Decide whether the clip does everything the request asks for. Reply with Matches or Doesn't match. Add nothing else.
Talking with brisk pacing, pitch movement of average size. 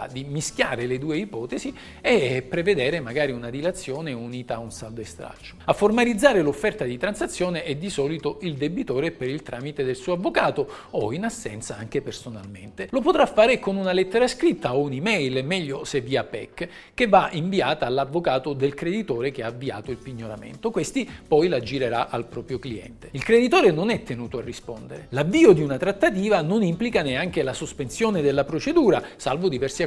Doesn't match